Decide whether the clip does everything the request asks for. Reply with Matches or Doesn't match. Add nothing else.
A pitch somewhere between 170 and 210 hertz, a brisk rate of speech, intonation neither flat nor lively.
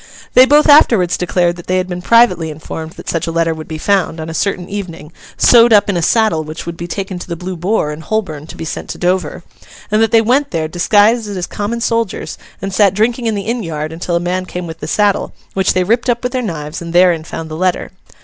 Matches